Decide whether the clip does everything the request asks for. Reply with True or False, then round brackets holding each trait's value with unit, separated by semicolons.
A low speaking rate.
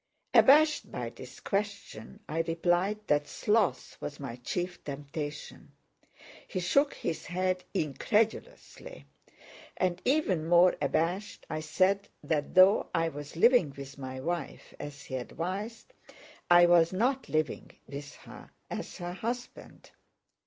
True (125 wpm)